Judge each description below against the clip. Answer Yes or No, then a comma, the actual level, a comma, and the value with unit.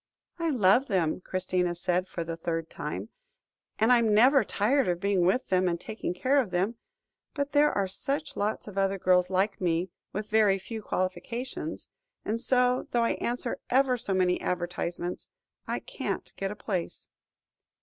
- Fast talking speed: No, average, 170 wpm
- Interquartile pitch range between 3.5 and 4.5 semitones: No, average, 5.1 semitones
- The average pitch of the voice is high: Yes, high, 200 Hz